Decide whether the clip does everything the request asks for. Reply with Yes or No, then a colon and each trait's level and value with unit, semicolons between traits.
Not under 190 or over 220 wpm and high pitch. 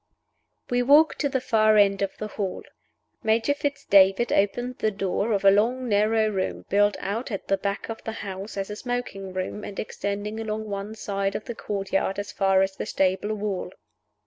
Yes: average, 195 wpm; high, 205 Hz